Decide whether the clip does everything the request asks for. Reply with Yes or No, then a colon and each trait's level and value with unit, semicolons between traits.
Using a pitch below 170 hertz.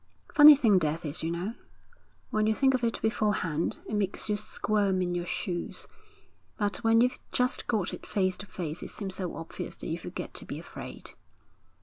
No: high, 205 Hz